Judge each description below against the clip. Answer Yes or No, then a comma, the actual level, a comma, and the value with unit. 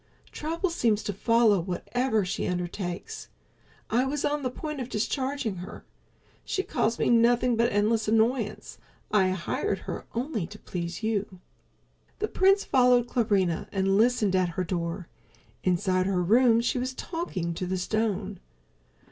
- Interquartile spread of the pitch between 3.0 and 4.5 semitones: No, average, 5.1 semitones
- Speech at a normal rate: Yes, average, 150 wpm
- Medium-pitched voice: No, high, 220 Hz